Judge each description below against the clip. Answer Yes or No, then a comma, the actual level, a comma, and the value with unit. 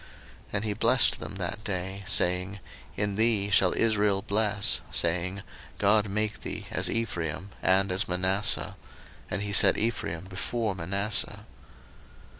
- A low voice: Yes, low, 100 Hz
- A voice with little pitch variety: Yes, narrow, 2.2 semitones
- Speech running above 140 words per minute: No, slow, 135 wpm